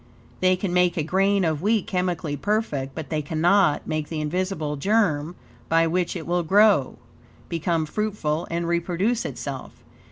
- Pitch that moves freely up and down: No, average, 3.7 semitones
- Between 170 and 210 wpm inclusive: No, average, 155 wpm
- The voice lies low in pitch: No, medium, 170 Hz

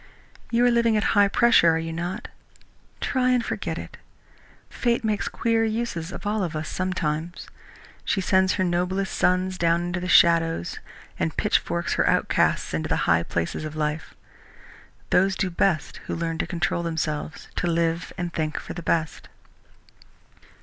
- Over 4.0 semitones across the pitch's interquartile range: No, average, 3.2 semitones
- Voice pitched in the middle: Yes, medium, 175 Hz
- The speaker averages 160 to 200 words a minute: Yes, average, 165 wpm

